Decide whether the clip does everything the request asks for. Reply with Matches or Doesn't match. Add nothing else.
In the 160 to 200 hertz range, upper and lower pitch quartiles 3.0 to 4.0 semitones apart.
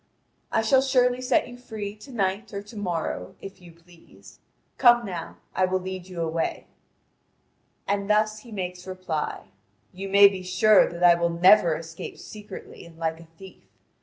Matches